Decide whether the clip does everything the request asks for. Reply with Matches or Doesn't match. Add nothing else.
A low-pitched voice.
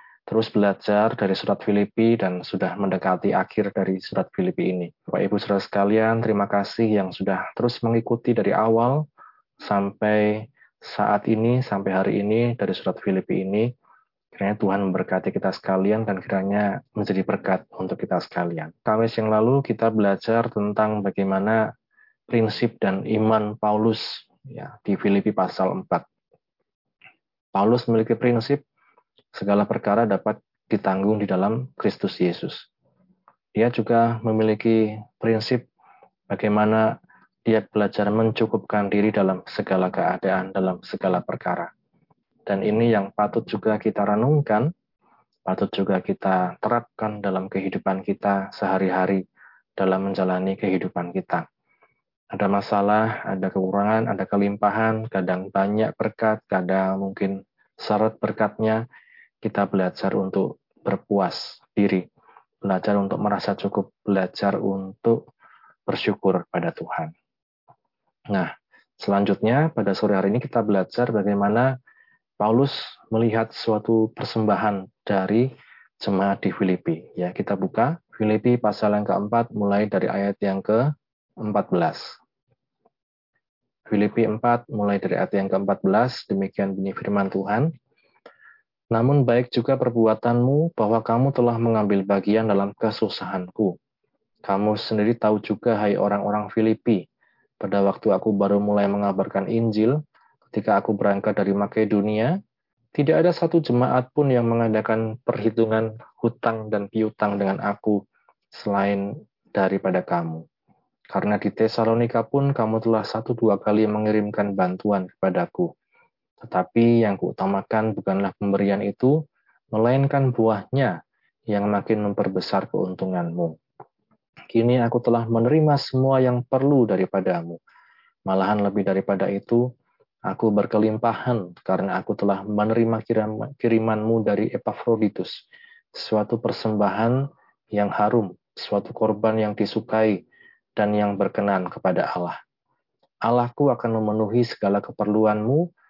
Matches